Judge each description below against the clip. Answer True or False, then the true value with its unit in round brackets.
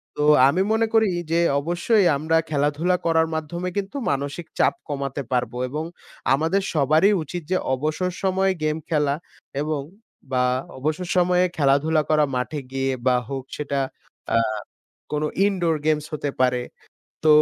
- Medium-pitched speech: True (155 Hz)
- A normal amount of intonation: True (3.8 semitones)